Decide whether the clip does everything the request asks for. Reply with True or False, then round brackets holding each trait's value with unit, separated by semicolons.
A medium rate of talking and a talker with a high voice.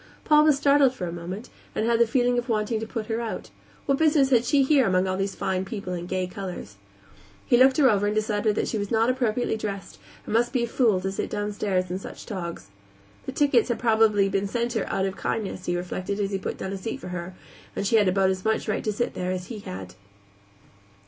False (240 wpm; 210 Hz)